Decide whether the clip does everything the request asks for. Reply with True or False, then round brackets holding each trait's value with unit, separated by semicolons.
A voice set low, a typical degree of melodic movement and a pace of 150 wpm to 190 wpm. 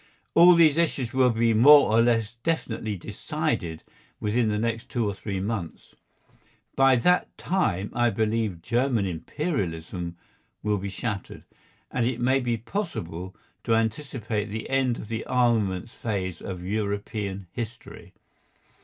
False (110 Hz; 3.8 semitones; 135 wpm)